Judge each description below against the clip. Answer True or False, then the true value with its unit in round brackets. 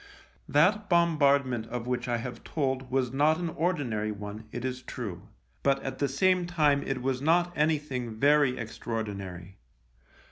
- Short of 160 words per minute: True (150 wpm)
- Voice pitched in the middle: False (130 Hz)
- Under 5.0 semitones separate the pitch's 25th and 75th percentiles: True (4.3 semitones)